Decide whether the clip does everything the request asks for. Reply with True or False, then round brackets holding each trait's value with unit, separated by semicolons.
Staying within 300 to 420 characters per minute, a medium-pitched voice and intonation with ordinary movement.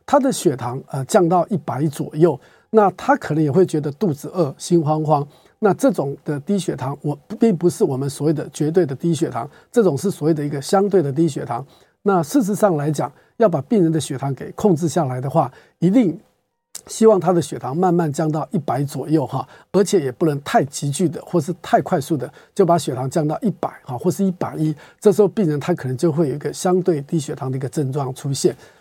True (315 characters per minute; 165 Hz; 4.1 semitones)